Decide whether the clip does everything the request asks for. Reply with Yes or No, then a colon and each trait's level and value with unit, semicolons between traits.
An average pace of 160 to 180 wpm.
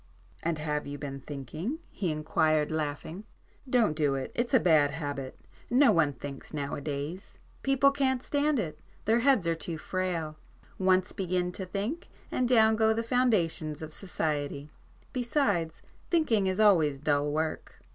No: average, 145 wpm